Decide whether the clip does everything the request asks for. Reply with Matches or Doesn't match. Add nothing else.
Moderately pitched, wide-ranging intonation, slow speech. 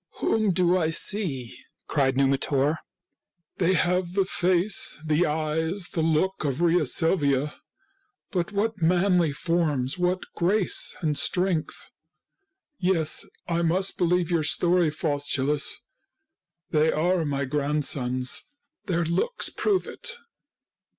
Doesn't match